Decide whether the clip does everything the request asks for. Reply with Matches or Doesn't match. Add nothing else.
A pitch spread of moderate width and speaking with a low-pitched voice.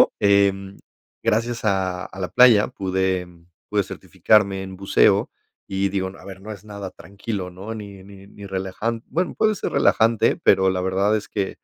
Doesn't match